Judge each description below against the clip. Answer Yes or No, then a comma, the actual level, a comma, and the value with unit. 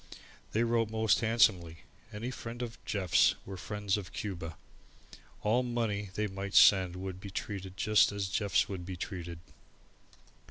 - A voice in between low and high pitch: No, low, 100 Hz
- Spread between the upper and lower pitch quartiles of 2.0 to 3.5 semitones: Yes, average, 2.9 semitones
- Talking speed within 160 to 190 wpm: No, average, 150 wpm